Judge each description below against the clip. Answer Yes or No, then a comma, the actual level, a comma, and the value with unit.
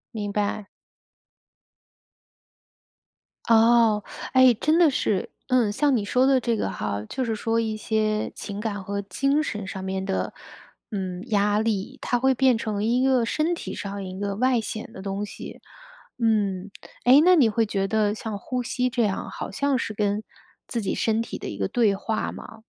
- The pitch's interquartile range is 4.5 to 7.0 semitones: No, average, 3.6 semitones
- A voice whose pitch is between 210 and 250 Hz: Yes, high, 220 Hz